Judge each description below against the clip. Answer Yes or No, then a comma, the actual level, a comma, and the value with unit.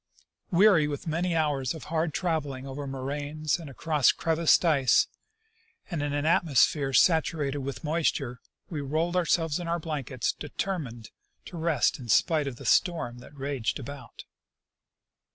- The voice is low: No, medium, 150 Hz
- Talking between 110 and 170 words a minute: Yes, average, 150 wpm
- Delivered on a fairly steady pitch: No, average, 3.2 semitones